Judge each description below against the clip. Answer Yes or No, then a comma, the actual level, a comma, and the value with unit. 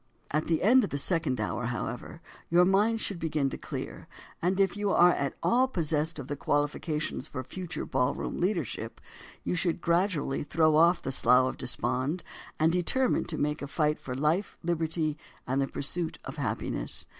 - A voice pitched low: No, medium, 160 Hz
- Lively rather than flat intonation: No, average, 3.9 semitones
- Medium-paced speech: Yes, average, 180 wpm